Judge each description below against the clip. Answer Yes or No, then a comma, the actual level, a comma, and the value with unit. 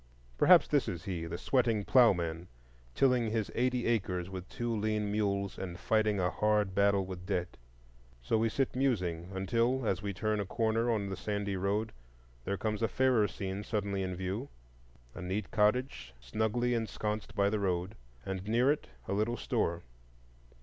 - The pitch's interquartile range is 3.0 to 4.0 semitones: Yes, average, 3.3 semitones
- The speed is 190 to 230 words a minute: No, average, 165 wpm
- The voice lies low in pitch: Yes, low, 100 Hz